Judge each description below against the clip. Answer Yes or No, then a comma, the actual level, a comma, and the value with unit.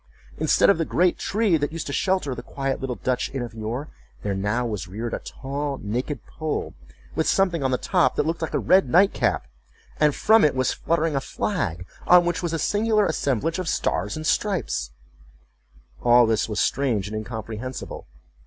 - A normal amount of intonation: No, wide, 6.5 semitones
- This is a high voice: No, medium, 140 Hz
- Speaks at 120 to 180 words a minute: No, average, 190 wpm